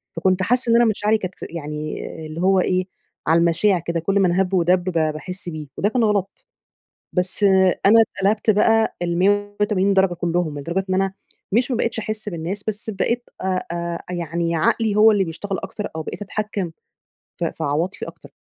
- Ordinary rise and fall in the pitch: Yes, average, 3.4 semitones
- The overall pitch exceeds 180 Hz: Yes, high, 190 Hz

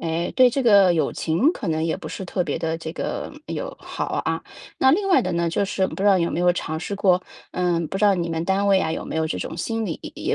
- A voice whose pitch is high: No, medium, 180 Hz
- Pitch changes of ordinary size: Yes, average, 3.6 semitones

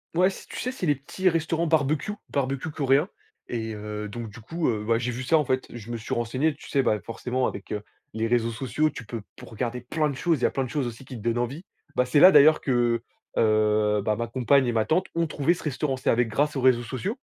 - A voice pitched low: Yes, low, 125 Hz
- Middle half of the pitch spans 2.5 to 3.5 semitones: No, average, 4.6 semitones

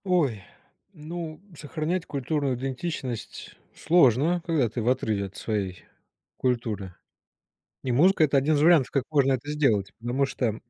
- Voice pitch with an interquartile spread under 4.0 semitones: No, average, 4.7 semitones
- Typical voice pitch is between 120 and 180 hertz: Yes, low, 135 Hz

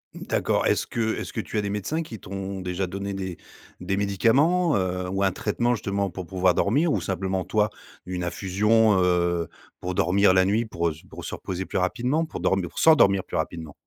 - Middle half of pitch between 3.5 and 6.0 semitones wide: No, average, 2.8 semitones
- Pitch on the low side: Yes, very low, 95 Hz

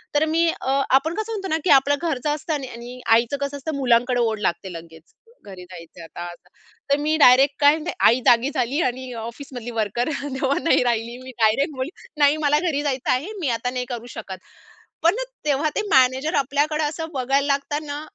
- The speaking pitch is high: Yes, very high, 270 Hz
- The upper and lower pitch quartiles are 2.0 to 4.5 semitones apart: Yes, average, 3.9 semitones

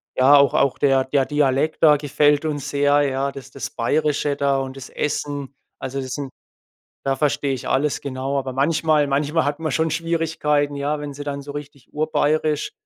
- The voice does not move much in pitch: Yes, narrow, 1.6 semitones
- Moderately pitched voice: Yes, medium, 145 Hz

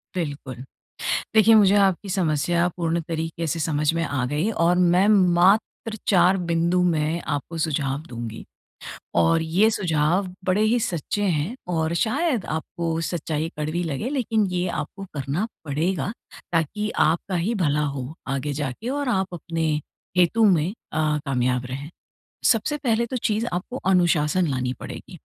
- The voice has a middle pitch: Yes, medium, 170 Hz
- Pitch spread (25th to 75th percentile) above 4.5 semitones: Yes, average, 5.0 semitones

